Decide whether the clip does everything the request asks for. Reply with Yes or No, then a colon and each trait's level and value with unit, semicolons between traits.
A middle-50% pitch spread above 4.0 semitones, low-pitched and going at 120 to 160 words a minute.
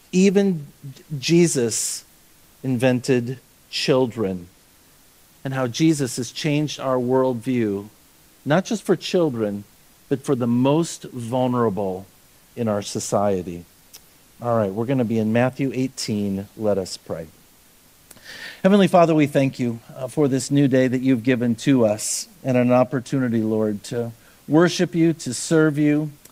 Yes: average, 4.7 semitones; low, 130 Hz; slow, 135 wpm